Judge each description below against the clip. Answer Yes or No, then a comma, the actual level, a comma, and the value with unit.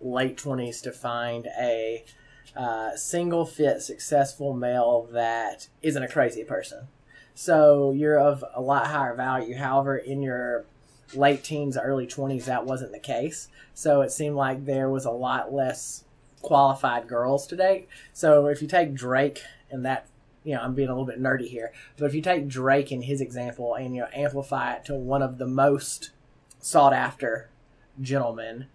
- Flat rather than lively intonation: Yes, narrow, 2.2 semitones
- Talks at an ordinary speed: Yes, average, 175 wpm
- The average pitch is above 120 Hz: Yes, low, 135 Hz